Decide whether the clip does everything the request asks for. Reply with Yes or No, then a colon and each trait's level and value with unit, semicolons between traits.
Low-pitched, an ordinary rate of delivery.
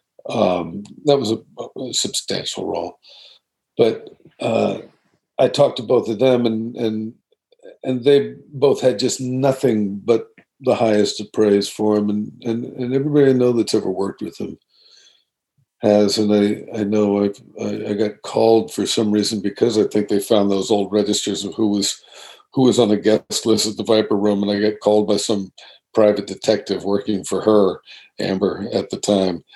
Yes: low, 110 Hz; average, 180 wpm